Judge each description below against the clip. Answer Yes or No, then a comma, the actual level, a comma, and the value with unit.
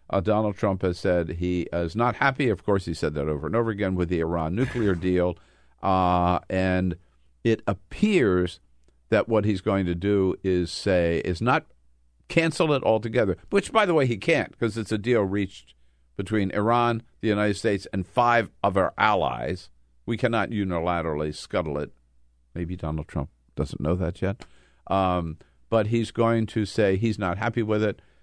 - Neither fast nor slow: Yes, average, 180 wpm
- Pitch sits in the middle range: No, very low, 95 Hz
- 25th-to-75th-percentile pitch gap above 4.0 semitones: Yes, average, 4.6 semitones